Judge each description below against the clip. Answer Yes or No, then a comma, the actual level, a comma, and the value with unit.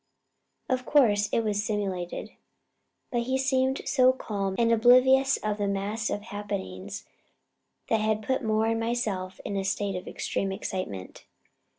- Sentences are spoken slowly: No, average, 150 wpm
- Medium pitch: No, high, 215 Hz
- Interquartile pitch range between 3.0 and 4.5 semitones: Yes, average, 3.7 semitones